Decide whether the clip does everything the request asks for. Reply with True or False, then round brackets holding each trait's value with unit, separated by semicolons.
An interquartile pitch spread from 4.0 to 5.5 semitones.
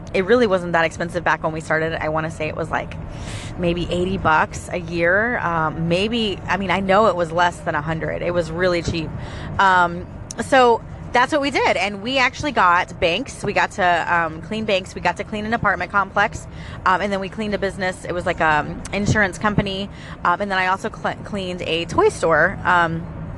False (3.3 semitones)